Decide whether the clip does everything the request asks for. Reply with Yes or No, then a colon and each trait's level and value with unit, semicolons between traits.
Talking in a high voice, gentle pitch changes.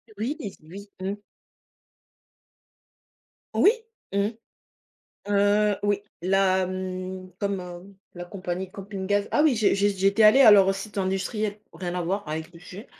Yes: high, 195 Hz; narrow, 1.8 semitones